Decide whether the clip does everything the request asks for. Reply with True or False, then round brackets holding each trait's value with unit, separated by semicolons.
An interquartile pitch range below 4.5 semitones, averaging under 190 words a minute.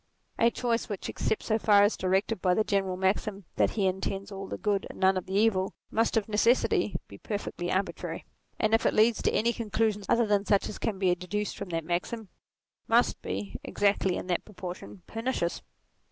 False (2.5 semitones; 195 wpm)